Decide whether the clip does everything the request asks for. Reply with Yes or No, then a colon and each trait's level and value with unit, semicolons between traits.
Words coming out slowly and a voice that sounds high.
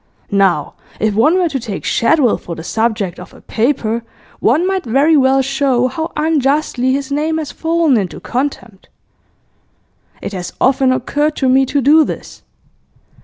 No: average, 160 wpm; very high, 265 Hz